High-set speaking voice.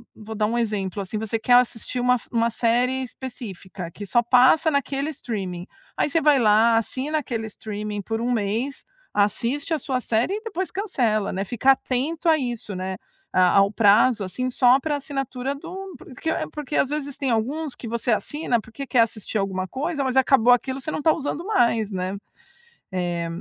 Yes: high, 245 Hz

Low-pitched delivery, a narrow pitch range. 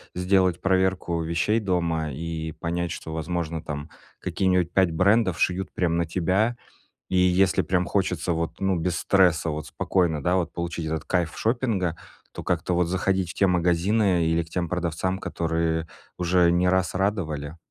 Yes: very low, 90 Hz; narrow, 2.2 semitones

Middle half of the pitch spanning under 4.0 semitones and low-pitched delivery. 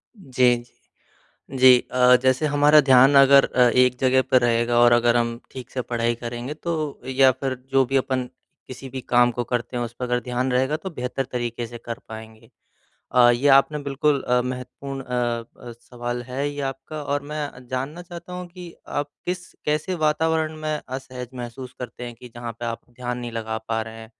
Yes: narrow, 2.6 semitones; low, 125 Hz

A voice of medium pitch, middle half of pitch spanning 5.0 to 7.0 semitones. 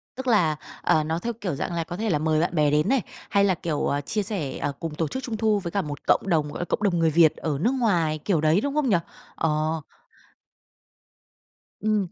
Yes: medium, 170 Hz; average, 5.3 semitones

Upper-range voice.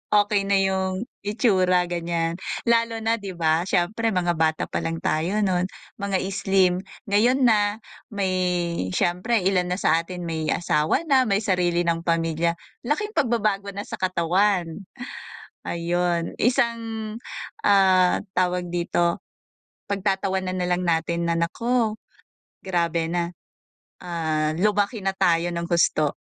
No: medium, 180 Hz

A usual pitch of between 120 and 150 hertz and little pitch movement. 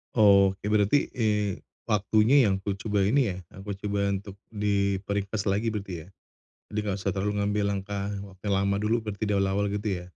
No: low, 100 Hz; narrow, 1.3 semitones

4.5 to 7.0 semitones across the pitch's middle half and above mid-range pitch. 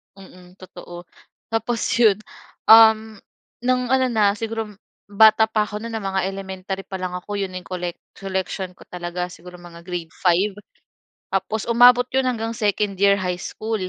No: average, 3.3 semitones; high, 200 Hz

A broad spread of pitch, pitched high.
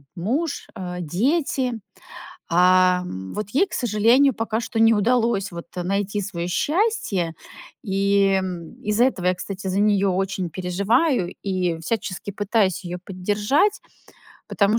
No: average, 3.8 semitones; high, 200 Hz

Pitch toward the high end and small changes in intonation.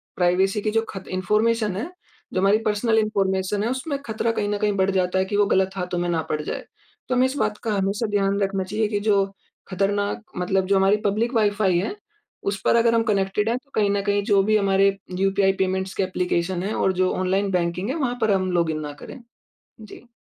Yes: high, 200 Hz; narrow, 2.3 semitones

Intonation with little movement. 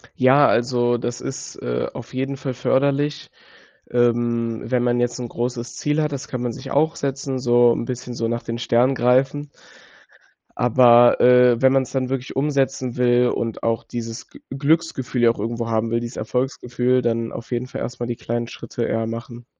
Yes: narrow, 2.0 semitones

